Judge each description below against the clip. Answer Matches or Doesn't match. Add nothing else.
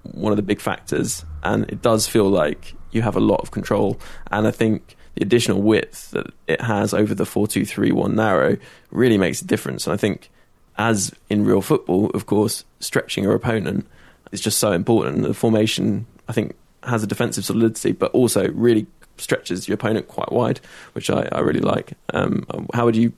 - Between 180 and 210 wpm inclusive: Matches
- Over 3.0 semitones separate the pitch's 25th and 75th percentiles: Doesn't match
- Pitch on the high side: Doesn't match